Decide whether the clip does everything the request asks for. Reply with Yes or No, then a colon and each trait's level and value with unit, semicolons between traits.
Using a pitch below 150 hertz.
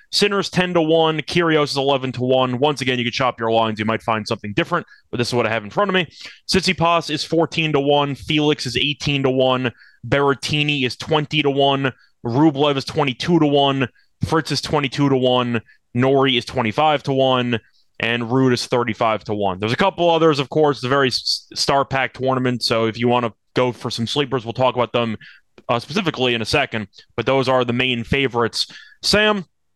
Yes: low, 135 Hz